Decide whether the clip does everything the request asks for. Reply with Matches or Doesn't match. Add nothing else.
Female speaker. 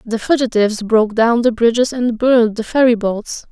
Matches